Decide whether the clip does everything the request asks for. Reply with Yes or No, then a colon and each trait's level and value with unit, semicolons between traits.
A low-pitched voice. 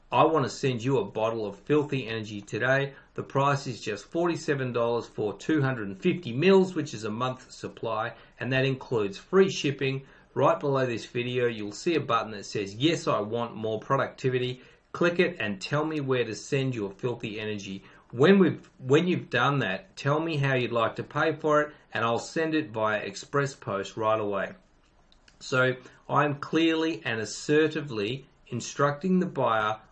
Yes: low, 130 Hz